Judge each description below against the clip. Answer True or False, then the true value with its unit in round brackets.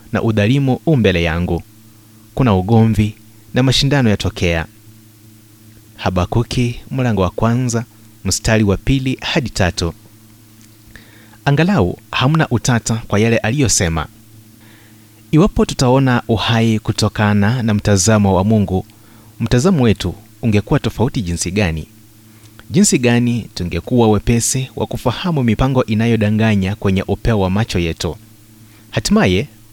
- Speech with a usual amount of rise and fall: False (2.1 semitones)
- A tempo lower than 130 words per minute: True (105 wpm)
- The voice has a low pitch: True (110 Hz)